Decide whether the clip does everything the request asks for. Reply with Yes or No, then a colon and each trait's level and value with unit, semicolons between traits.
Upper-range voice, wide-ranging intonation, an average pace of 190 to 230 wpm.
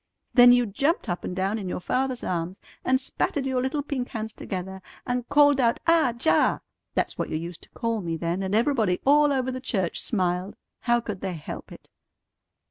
Yes: high, 230 Hz; wide, 5.8 semitones; average, 200 wpm